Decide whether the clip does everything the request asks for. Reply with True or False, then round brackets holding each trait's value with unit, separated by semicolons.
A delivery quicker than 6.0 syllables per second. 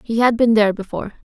True (7.5 syllables/s)